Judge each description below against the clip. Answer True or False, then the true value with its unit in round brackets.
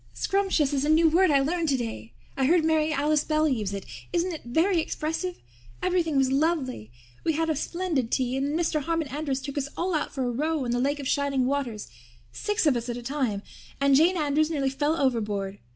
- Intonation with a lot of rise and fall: False (3.7 semitones)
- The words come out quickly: True (215 wpm)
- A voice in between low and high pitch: False (290 Hz)